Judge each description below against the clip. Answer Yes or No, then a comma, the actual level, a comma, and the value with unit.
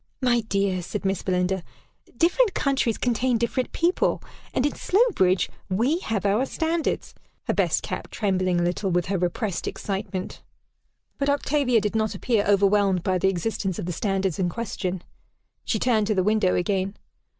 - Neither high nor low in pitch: No, high, 205 Hz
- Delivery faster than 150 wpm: Yes, average, 160 wpm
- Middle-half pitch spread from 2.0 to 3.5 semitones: No, average, 4.6 semitones